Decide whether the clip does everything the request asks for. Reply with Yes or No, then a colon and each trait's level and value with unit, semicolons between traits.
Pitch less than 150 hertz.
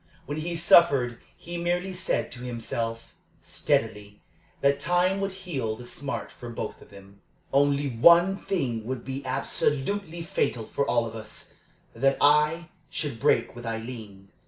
Yes: low, 135 Hz